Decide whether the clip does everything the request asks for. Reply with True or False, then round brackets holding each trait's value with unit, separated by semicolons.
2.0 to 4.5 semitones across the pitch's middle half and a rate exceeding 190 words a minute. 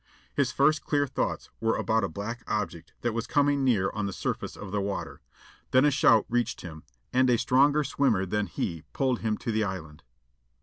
False (4.9 semitones; 200 wpm)